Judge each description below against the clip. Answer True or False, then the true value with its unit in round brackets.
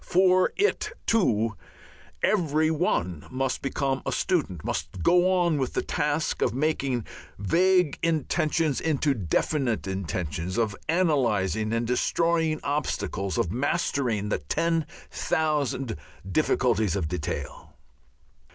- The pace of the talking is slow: True (115 wpm)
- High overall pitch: False (135 Hz)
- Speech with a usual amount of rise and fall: False (7.6 semitones)